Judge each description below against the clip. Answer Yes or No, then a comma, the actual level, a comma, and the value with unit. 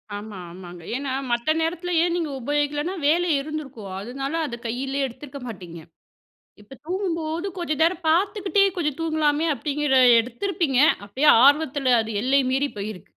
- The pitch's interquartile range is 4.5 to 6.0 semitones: Yes, average, 4.8 semitones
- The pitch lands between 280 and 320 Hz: Yes, very high, 290 Hz